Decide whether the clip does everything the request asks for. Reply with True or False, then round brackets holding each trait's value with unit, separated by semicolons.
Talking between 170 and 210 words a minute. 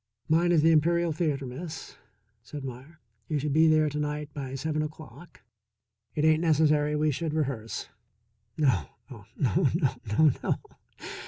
False (155 wpm)